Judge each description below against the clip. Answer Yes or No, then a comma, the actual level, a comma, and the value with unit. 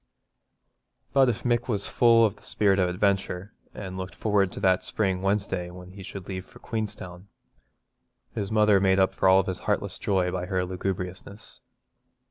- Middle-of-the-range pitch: No, very low, 95 Hz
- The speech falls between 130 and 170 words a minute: Yes, average, 165 wpm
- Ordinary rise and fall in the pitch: No, narrow, 2.0 semitones